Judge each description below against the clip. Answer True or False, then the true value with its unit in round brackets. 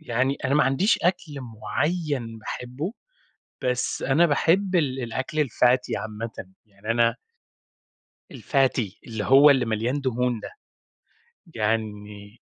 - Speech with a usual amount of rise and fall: True (4.2 semitones)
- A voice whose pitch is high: False (125 Hz)